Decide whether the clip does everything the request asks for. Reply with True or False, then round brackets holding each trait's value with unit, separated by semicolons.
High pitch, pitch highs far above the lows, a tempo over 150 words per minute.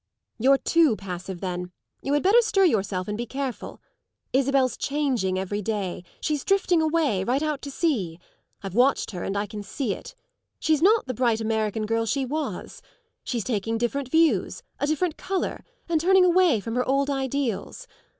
True (260 Hz; 6.7 semitones; 175 wpm)